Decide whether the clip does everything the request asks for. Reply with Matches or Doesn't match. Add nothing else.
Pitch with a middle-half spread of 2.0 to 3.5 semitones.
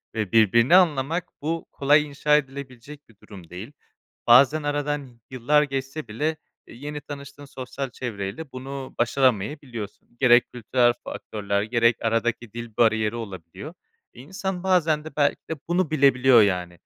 Doesn't match